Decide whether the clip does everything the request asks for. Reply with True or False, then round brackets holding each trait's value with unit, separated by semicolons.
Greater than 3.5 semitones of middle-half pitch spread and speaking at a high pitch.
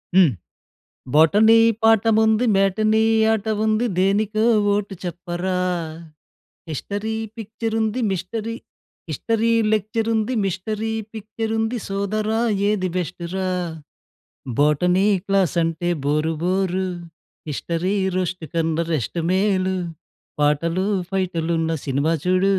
True (3.9 semitones; 195 Hz)